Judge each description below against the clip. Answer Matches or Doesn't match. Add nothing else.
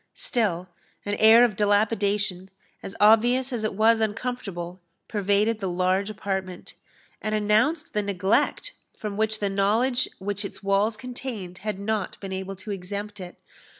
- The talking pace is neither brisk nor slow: Matches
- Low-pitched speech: Doesn't match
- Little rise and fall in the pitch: Matches